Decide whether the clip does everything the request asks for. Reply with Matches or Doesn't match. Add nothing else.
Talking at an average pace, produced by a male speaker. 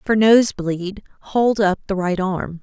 Doesn't match